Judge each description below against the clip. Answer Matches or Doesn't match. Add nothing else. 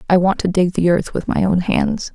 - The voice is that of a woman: Matches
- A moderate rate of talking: Doesn't match